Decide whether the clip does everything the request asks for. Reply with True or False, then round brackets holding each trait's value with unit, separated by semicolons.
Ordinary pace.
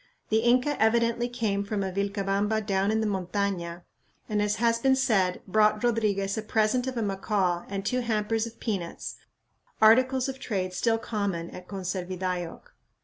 True (160 wpm)